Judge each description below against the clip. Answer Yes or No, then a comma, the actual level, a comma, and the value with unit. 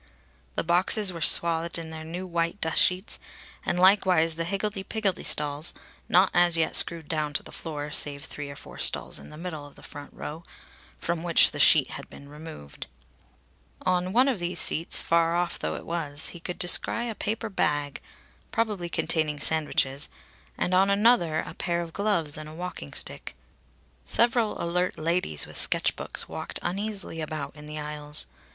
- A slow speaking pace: No, average, 175 wpm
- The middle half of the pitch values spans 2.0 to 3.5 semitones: Yes, average, 3.2 semitones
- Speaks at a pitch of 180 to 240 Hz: No, medium, 170 Hz